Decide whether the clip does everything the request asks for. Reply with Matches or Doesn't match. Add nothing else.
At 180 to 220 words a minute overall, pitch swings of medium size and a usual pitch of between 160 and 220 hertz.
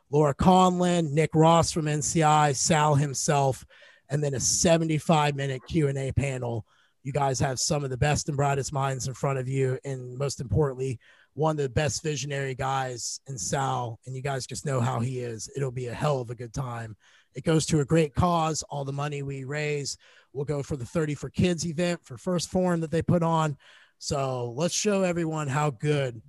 Doesn't match